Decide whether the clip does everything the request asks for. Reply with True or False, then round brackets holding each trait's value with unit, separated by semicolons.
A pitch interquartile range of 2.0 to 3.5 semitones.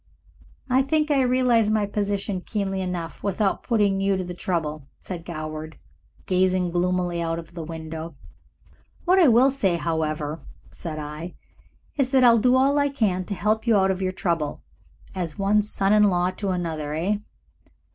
False (4.4 semitones)